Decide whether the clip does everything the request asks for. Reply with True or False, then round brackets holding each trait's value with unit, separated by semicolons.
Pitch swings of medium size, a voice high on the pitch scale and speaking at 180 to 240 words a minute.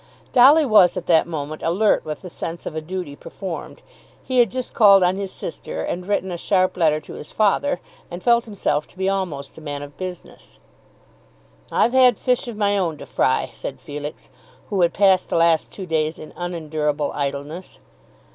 False (4.5 semitones; 180 Hz; 190 wpm)